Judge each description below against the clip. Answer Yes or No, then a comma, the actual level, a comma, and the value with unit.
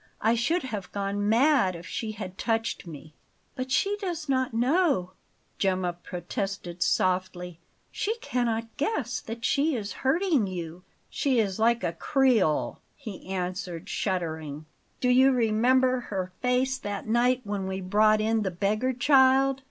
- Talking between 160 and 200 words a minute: No, average, 145 wpm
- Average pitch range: No, wide, 5.7 semitones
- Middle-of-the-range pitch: No, high, 220 Hz